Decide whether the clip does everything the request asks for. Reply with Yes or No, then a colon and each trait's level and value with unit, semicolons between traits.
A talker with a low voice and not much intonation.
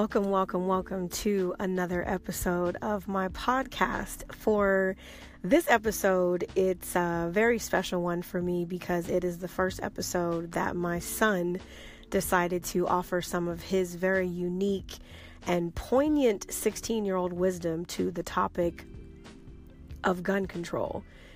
No: medium, 185 Hz; narrow, 1.7 semitones